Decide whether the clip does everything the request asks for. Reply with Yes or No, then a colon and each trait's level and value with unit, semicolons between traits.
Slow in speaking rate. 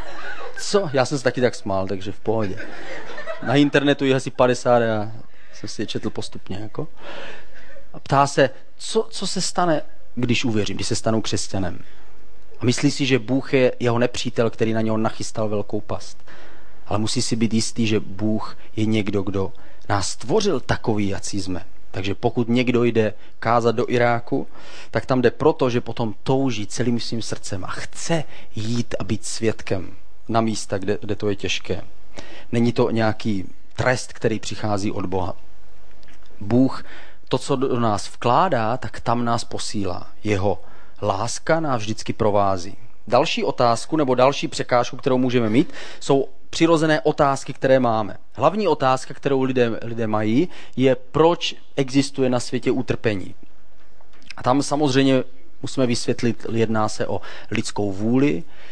No: average, 155 wpm